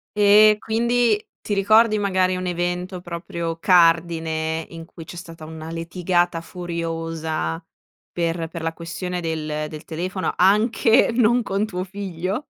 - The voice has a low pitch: No, medium, 175 Hz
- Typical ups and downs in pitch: Yes, average, 3.2 semitones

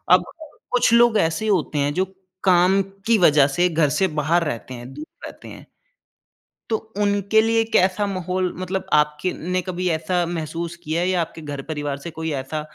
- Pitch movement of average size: Yes, average, 3.7 semitones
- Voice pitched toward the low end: No, medium, 175 Hz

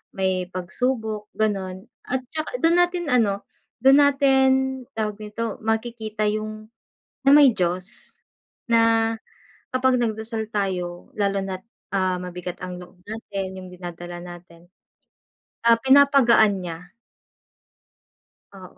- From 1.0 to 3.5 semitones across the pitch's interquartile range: No, average, 4.2 semitones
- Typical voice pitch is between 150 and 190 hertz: No, high, 215 Hz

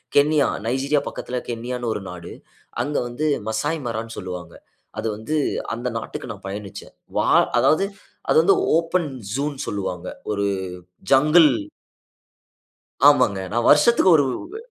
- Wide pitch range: Yes, wide, 5.8 semitones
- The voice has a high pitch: No, low, 125 Hz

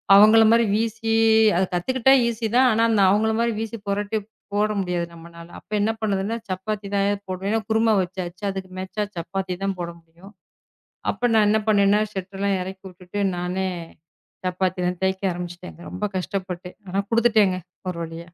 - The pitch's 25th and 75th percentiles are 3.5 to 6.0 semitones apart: No, average, 3.0 semitones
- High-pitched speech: Yes, high, 195 Hz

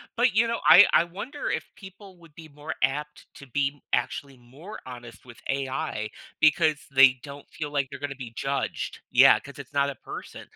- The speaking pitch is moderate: Yes, medium, 145 Hz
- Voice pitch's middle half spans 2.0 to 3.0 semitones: No, average, 3.8 semitones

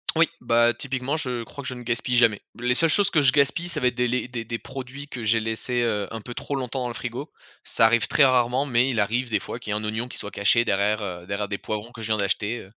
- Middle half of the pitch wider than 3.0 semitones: No, average, 2.7 semitones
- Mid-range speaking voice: No, low, 120 Hz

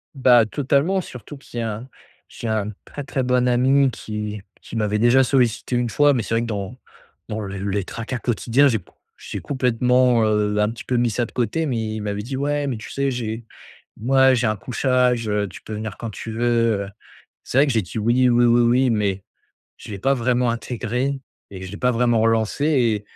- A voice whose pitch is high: No, low, 120 Hz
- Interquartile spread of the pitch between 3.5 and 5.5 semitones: No, average, 2.9 semitones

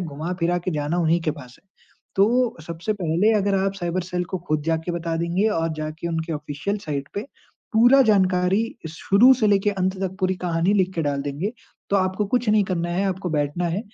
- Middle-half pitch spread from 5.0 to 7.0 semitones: No, average, 3.3 semitones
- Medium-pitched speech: Yes, medium, 180 Hz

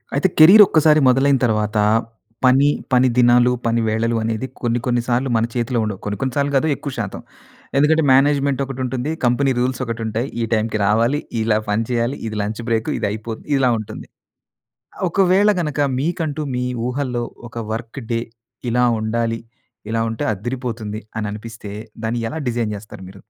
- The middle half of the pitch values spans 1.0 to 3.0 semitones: No, average, 3.5 semitones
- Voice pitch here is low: Yes, low, 120 Hz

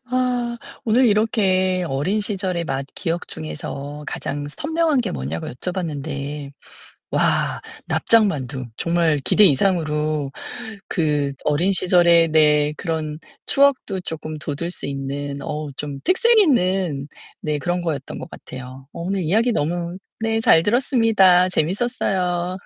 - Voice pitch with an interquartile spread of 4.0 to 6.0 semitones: Yes, average, 5.3 semitones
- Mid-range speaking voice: Yes, medium, 170 Hz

